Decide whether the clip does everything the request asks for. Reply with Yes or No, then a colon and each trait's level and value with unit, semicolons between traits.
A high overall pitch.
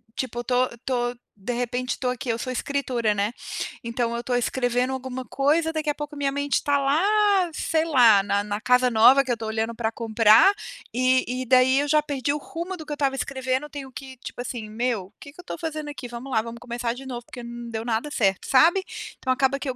Yes: very high, 255 Hz